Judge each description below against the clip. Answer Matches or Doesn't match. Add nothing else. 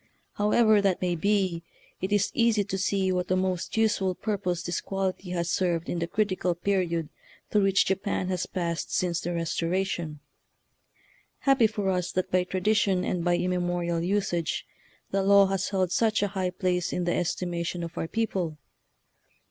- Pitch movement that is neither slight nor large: Doesn't match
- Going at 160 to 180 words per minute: Matches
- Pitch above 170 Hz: Matches